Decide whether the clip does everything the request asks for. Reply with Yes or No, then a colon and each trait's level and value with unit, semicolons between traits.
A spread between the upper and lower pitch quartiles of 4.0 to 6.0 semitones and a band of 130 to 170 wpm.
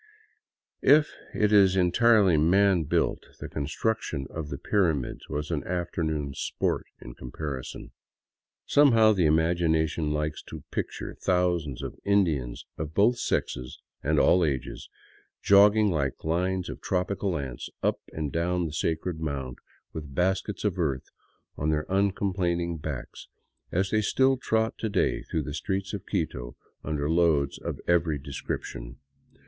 Yes: average, 4.6 semitones; average, 140 wpm